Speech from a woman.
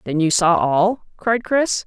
Yes: female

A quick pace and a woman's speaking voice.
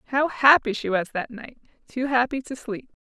No: average, 180 wpm; female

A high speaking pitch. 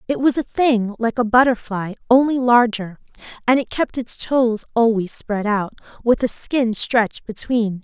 Yes: high, 235 Hz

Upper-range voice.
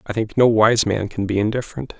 No: low, 110 Hz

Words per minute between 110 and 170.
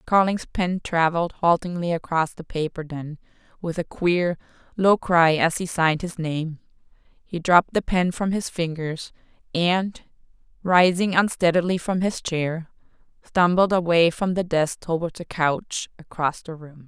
Yes: average, 150 wpm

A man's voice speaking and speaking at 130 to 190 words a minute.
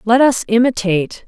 No: female; average, 140 wpm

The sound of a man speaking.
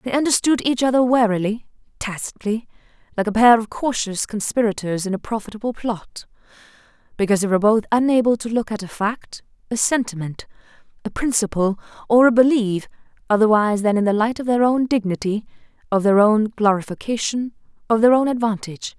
No: female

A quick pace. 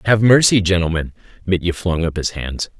No: average, 170 wpm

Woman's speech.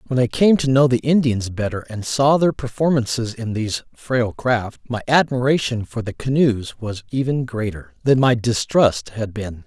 No: male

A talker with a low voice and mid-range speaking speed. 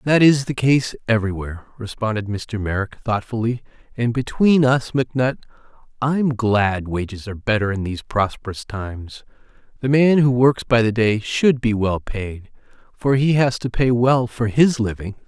Yes: low, 115 Hz; average, 165 wpm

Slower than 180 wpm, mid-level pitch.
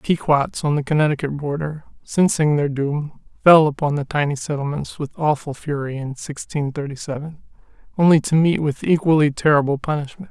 Yes: average, 165 wpm; medium, 150 Hz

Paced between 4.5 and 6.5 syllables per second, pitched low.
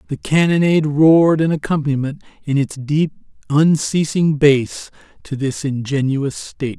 No: 4.9 syllables/s; medium, 145 Hz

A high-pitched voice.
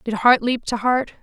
Yes: high, 235 Hz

